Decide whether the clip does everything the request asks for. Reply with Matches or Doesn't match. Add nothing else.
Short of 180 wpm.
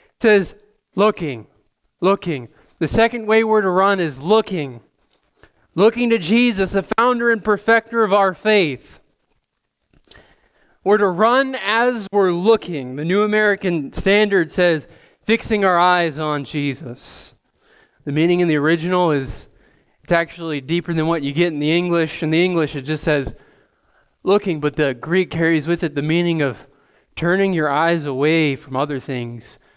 Matches